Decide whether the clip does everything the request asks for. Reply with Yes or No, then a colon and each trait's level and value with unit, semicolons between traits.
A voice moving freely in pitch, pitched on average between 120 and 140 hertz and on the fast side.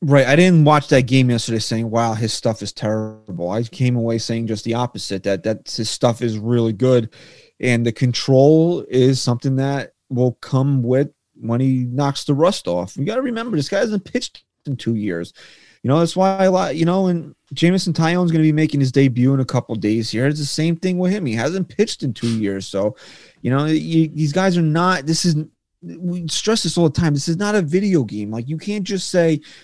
Yes: wide, 6.4 semitones; low, 135 Hz; fast, 235 wpm